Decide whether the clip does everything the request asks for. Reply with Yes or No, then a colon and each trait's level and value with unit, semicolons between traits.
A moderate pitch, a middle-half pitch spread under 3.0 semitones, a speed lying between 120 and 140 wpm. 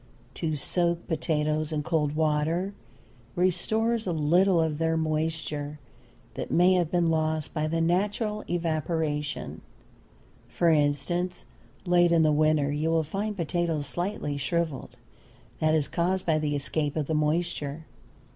Yes: medium, 160 Hz; narrow, 2.5 semitones; slow, 135 wpm